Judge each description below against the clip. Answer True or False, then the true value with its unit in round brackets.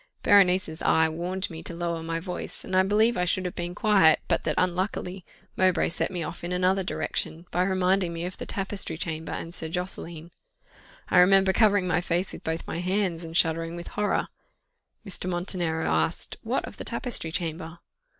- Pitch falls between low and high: True (180 Hz)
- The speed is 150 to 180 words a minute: False (190 wpm)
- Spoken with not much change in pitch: True (2.2 semitones)